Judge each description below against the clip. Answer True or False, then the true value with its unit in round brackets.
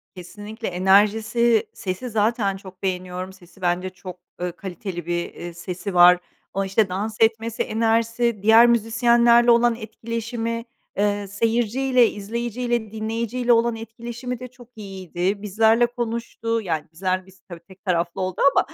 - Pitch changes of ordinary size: True (3.7 semitones)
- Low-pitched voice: False (215 Hz)